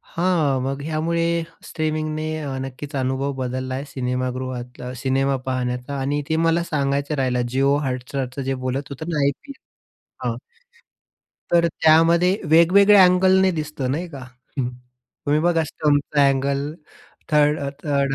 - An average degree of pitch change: Yes, average, 3.3 semitones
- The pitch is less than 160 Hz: Yes, medium, 140 Hz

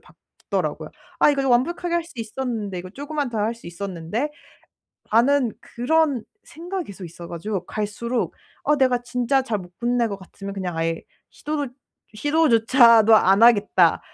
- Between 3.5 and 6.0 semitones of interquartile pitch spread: Yes, wide, 5.6 semitones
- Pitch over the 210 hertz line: Yes, high, 235 Hz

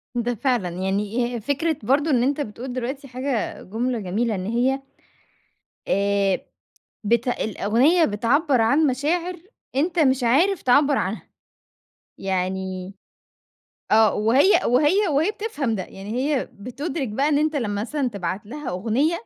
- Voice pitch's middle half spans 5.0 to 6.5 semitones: Yes, wide, 5.5 semitones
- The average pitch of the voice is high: Yes, high, 245 Hz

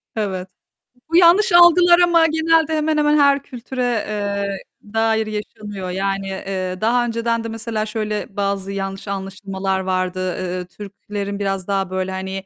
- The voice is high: Yes, high, 205 Hz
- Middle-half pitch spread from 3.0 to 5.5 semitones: Yes, average, 4.2 semitones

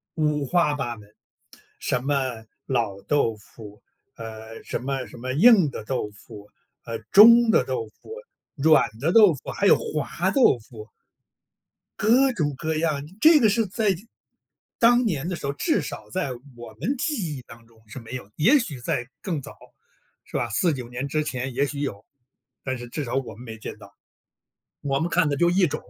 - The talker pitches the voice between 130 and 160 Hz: Yes, medium, 140 Hz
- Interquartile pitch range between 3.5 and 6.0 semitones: No, wide, 7.1 semitones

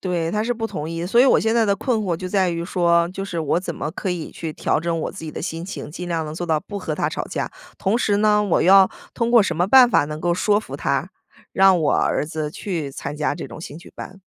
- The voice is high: No, medium, 180 Hz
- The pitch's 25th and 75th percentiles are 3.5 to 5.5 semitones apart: Yes, average, 3.9 semitones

